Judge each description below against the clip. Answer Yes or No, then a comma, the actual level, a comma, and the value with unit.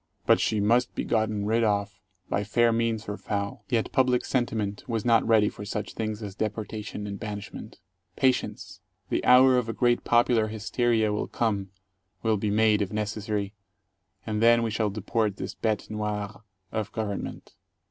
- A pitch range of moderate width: No, narrow, 1.8 semitones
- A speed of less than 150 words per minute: No, average, 170 wpm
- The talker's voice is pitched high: No, low, 110 Hz